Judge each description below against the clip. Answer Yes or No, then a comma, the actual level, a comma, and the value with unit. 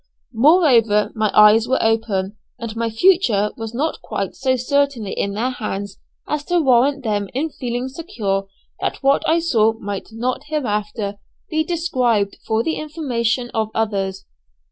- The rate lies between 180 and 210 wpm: No, average, 150 wpm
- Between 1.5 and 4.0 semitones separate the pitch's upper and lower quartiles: No, average, 5.0 semitones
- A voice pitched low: No, high, 230 Hz